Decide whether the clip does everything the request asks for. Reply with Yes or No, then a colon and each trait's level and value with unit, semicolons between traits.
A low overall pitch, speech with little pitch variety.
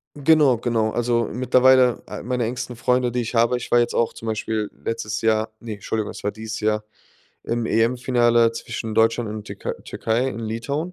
Yes: low, 115 Hz; narrow, 2.0 semitones